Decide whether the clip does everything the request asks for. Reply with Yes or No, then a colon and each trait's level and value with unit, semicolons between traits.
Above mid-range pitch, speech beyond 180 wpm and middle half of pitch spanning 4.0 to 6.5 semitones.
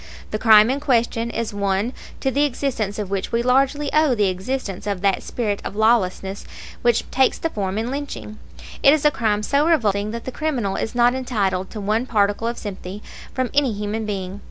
Yes: high, 225 Hz; average, 195 wpm; average, 4.3 semitones